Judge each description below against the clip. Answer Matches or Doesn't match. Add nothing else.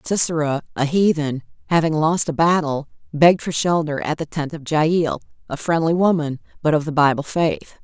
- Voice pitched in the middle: Matches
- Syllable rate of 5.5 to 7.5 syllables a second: Doesn't match